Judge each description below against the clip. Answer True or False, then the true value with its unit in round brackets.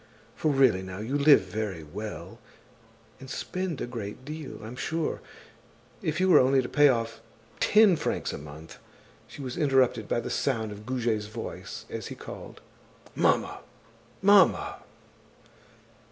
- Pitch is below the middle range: True (125 Hz)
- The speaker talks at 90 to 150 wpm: True (145 wpm)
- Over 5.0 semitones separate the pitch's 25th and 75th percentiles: True (5.5 semitones)